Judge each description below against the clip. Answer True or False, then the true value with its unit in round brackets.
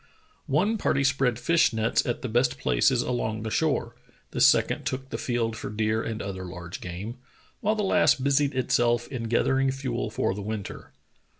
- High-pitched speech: False (120 Hz)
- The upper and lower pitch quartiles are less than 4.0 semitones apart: True (3.5 semitones)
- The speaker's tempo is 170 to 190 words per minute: True (180 wpm)